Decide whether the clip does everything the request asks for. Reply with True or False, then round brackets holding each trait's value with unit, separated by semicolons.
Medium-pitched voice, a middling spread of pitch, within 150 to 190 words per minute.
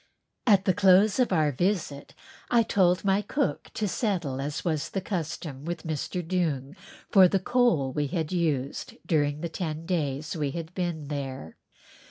True (165 Hz; 4.4 semitones; 165 wpm)